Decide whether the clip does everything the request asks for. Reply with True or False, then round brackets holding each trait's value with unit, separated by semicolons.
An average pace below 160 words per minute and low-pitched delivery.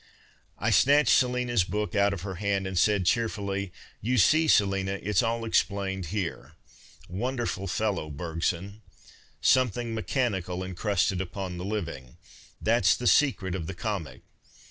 True (145 wpm; 100 Hz)